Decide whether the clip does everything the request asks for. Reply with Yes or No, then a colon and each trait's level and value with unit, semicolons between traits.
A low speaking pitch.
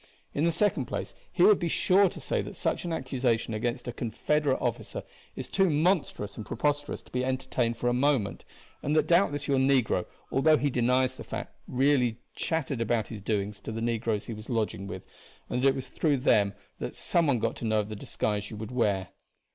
Yes: low, 125 Hz